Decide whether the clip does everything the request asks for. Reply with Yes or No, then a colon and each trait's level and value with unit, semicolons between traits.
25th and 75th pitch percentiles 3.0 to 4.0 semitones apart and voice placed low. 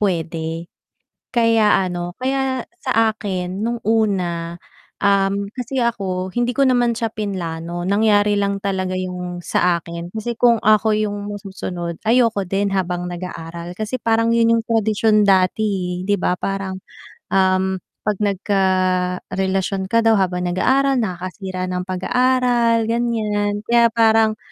No: average, 3.6 semitones; high, 200 Hz